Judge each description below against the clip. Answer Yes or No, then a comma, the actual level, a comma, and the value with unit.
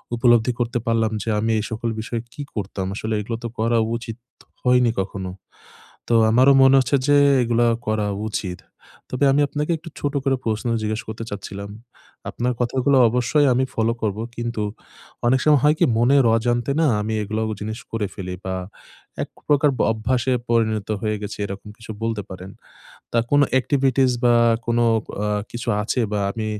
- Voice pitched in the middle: No, low, 115 Hz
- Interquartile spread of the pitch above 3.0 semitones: No, average, 2.7 semitones